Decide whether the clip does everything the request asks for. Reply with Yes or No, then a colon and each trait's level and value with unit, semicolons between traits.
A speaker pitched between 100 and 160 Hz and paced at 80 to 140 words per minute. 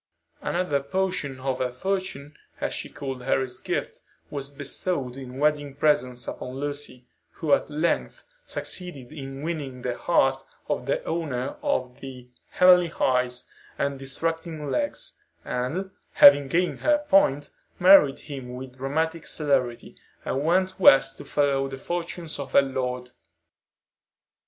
Yes: medium, 140 Hz; slow, 135 wpm